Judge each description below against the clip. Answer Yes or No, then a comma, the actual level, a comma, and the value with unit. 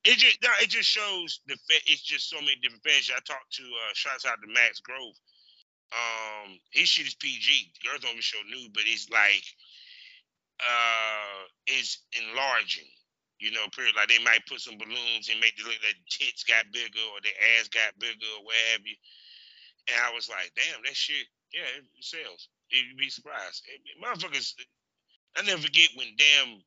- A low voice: Yes, low, 115 Hz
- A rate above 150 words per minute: Yes, average, 185 wpm